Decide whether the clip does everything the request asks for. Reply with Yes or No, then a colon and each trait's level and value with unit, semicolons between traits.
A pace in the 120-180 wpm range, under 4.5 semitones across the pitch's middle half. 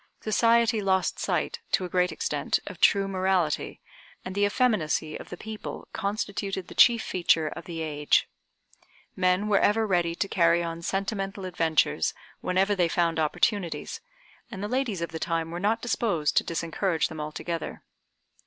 Yes: average, 160 wpm; average, 3.4 semitones